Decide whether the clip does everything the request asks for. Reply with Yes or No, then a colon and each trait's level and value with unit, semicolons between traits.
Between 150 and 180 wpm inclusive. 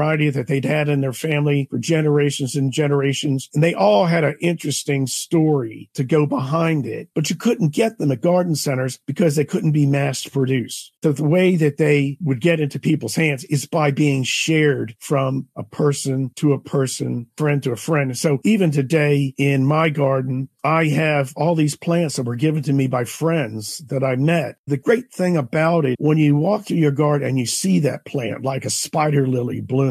No: fast, 205 wpm